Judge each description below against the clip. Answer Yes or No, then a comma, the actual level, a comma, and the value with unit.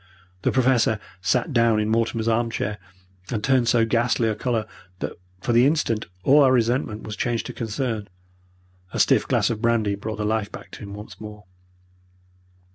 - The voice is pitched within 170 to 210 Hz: No, low, 115 Hz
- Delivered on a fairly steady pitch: Yes, narrow, 2.1 semitones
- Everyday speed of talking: Yes, average, 180 wpm